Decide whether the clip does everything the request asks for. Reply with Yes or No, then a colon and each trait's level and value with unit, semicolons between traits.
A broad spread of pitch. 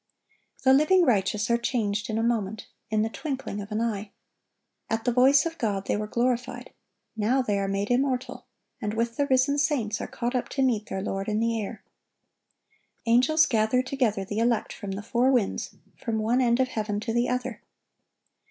No: average, 3.3 semitones